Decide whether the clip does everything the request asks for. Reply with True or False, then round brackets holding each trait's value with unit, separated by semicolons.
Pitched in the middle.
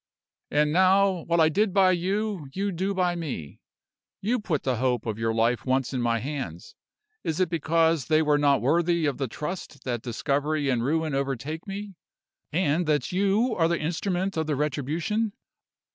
True (160 Hz)